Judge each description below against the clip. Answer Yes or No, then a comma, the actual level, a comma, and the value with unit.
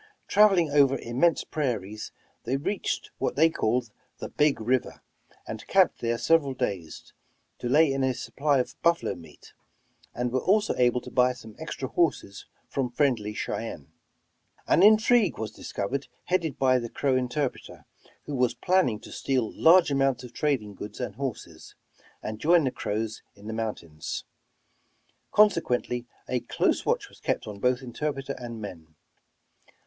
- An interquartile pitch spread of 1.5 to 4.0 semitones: No, average, 4.8 semitones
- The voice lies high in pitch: No, low, 125 Hz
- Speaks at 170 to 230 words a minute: No, average, 155 wpm